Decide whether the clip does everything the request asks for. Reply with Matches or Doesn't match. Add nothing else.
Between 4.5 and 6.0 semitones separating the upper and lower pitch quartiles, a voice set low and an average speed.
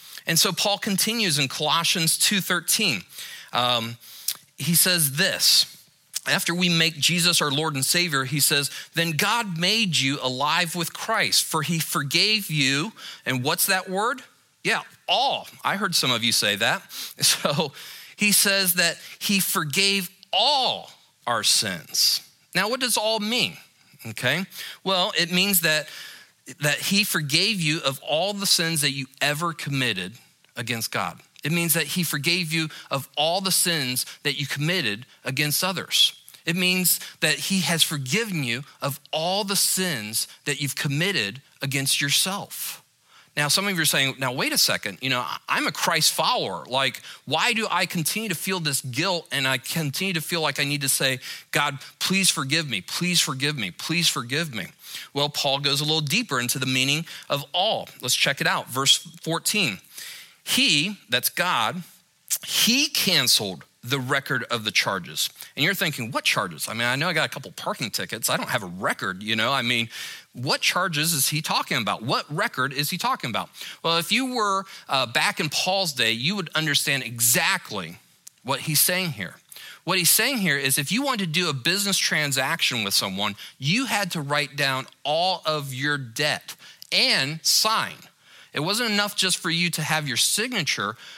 Doesn't match